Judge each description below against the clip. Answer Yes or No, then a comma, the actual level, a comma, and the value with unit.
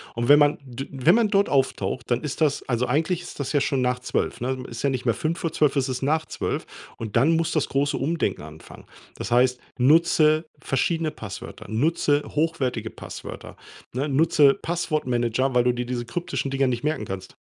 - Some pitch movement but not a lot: Yes, average, 4.0 semitones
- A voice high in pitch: No, low, 135 Hz